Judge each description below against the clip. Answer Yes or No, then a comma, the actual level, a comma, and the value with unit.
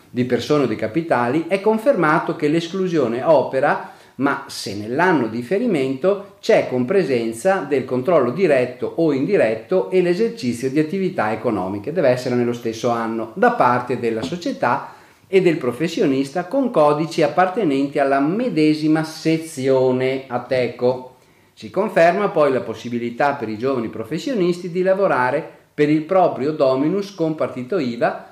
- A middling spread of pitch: No, wide, 6.2 semitones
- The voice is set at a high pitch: No, medium, 145 Hz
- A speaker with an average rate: Yes, average, 140 wpm